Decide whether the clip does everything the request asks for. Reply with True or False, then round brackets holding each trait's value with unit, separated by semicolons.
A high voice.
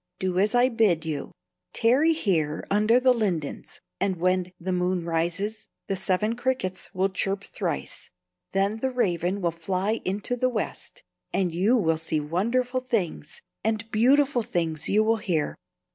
True (195 Hz)